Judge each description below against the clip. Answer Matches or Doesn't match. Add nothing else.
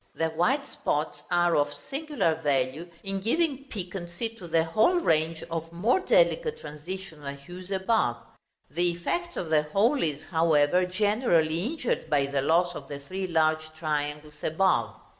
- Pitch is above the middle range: Doesn't match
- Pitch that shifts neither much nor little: Matches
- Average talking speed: Matches